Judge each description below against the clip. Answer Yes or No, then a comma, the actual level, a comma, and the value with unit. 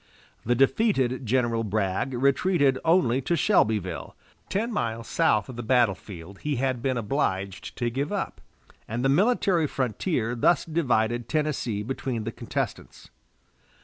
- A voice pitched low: Yes, low, 125 Hz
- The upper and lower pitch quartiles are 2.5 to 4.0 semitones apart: No, average, 4.9 semitones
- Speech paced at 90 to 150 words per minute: Yes, average, 140 wpm